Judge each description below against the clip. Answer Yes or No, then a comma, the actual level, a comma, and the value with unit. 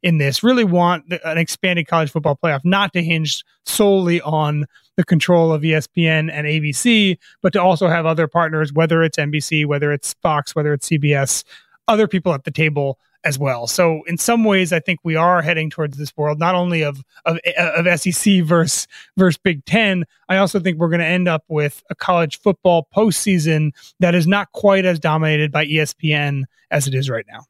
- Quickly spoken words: No, average, 195 wpm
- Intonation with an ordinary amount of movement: Yes, average, 3.0 semitones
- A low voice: No, medium, 165 Hz